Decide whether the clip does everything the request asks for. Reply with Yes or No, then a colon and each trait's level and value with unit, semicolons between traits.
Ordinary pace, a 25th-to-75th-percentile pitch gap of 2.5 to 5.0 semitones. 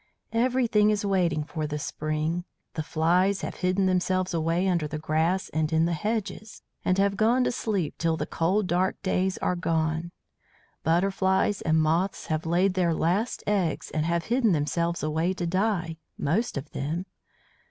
Yes: average, 165 wpm; average, 3.4 semitones